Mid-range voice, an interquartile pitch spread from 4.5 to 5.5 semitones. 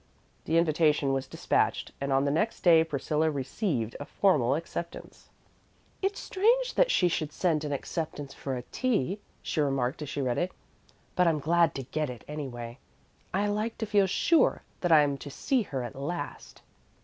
Yes: medium, 155 Hz; average, 4.9 semitones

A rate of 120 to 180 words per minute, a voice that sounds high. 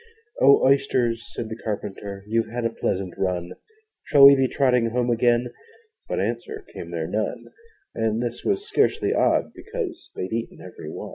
No: average, 160 wpm; low, 120 Hz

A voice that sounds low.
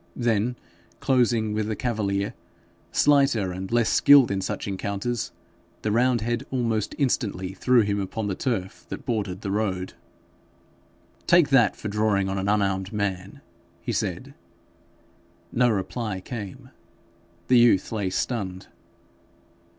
Yes: low, 105 Hz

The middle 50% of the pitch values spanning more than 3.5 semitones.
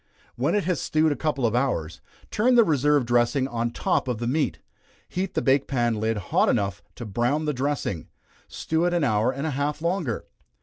Yes: average, 4.7 semitones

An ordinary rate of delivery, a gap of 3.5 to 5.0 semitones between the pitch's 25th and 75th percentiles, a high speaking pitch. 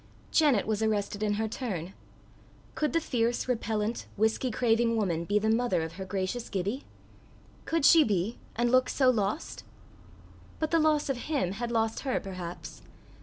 Yes: average, 165 wpm; average, 4.1 semitones; high, 225 Hz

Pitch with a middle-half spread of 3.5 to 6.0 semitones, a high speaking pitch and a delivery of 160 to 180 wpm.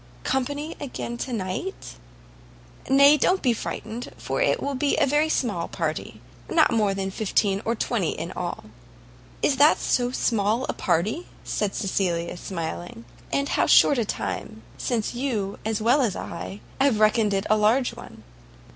Yes: wide, 5.5 semitones; high, 225 Hz; average, 165 wpm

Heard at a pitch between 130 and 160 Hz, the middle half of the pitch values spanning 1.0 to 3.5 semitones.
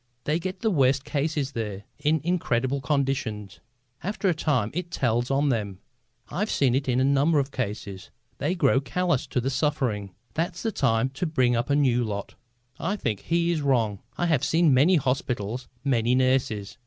No: low, 135 Hz; average, 4.8 semitones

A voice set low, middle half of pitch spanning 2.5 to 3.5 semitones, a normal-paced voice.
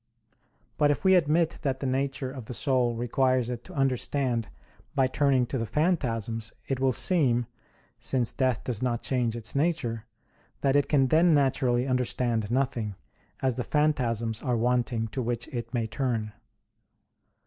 Yes: low, 125 Hz; average, 2.8 semitones; average, 160 wpm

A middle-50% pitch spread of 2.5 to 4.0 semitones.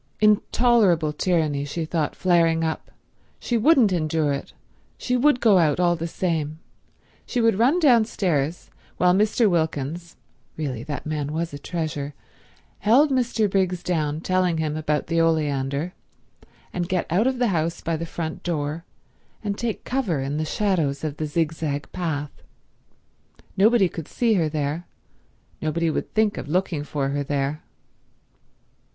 No: average, 4.5 semitones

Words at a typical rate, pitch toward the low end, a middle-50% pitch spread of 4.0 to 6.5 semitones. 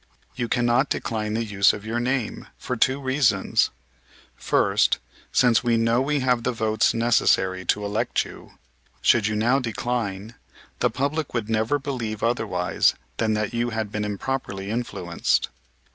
No: average, 150 wpm; low, 115 Hz; average, 2.7 semitones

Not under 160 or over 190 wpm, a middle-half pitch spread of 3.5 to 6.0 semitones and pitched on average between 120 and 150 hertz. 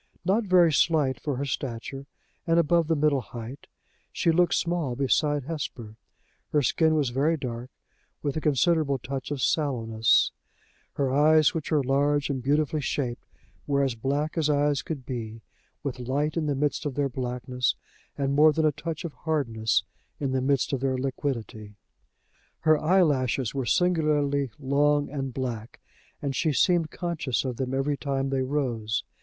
No: average, 165 wpm; average, 2.9 semitones; medium, 140 Hz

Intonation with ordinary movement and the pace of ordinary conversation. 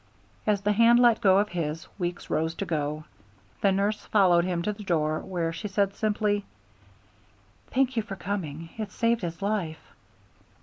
Yes: average, 3.9 semitones; average, 170 wpm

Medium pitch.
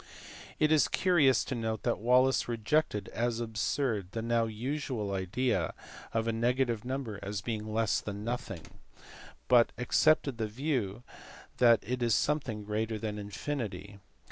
No: low, 115 Hz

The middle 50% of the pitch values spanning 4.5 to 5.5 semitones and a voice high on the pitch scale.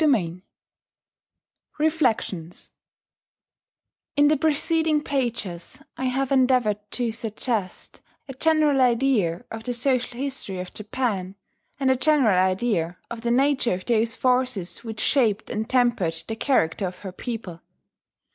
Yes: average, 5.0 semitones; high, 240 Hz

